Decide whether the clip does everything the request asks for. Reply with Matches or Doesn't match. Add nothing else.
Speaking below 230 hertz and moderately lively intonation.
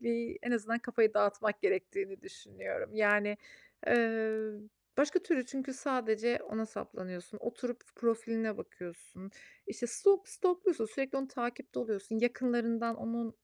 Doesn't match